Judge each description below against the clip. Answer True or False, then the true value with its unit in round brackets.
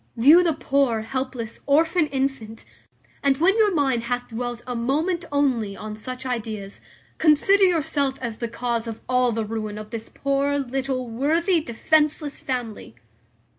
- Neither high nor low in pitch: False (260 Hz)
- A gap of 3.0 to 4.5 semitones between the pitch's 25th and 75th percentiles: True (4.2 semitones)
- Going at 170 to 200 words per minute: False (150 wpm)